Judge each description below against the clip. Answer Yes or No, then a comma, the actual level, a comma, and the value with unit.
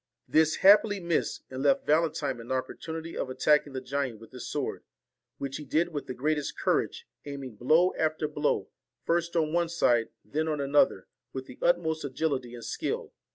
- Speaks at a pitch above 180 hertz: No, medium, 150 Hz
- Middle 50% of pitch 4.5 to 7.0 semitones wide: No, average, 3.6 semitones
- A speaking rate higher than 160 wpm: Yes, average, 180 wpm